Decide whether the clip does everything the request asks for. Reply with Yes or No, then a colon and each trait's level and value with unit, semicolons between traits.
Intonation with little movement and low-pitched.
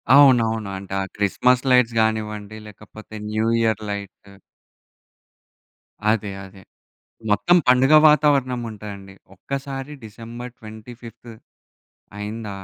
No: average, 3.3 semitones; low, 110 Hz